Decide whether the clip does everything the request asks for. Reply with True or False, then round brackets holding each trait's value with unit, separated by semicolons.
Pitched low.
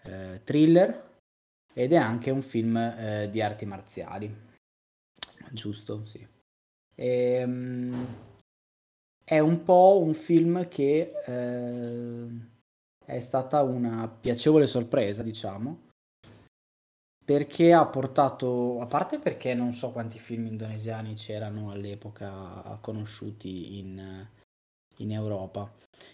True (115 Hz)